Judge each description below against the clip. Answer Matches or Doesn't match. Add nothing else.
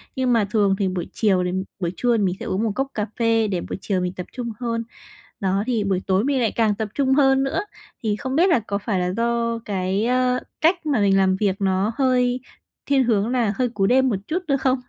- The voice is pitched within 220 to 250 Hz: Matches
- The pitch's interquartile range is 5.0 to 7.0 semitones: Doesn't match